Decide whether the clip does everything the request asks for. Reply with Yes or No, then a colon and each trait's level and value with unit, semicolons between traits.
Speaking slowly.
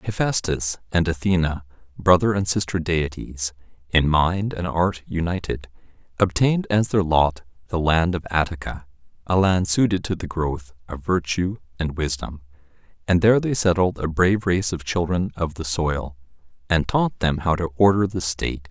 No: average, 160 wpm